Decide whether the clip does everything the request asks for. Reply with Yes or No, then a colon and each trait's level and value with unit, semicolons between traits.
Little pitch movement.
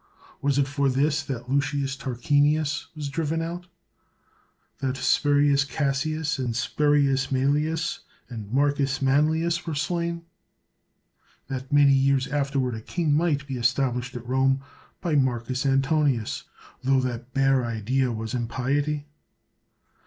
Yes: narrow, 2.2 semitones